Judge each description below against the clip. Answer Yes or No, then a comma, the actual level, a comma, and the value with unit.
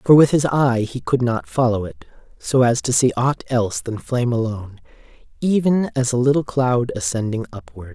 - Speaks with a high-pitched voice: No, low, 125 Hz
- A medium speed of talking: Yes, average, 190 wpm